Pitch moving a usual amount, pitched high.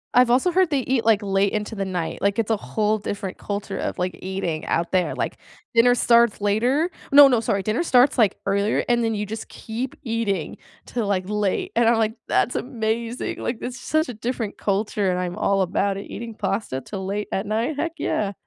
Yes: average, 3.1 semitones; high, 215 Hz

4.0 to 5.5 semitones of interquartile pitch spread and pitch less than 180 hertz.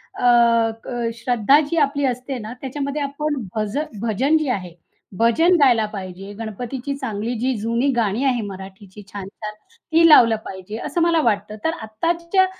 No: average, 5.0 semitones; high, 240 Hz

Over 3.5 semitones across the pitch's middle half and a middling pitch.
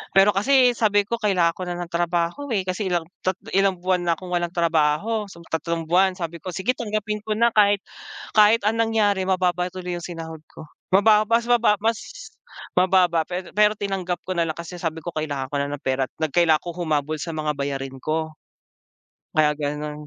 Yes: average, 4.0 semitones; medium, 180 Hz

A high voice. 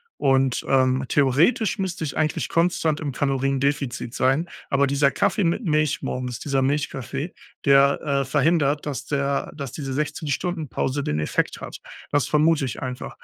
No: medium, 140 Hz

